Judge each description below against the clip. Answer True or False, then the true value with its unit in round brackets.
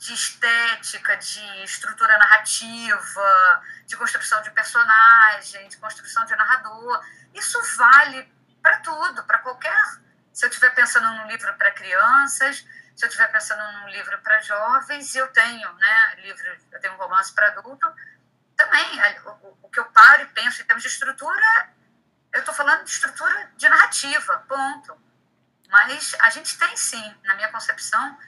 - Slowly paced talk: False (155 wpm)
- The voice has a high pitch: True (270 Hz)